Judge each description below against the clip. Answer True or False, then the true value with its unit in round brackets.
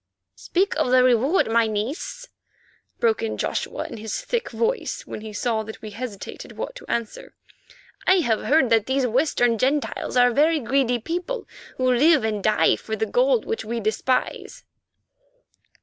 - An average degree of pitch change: False (7.0 semitones)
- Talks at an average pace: True (165 wpm)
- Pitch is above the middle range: True (255 Hz)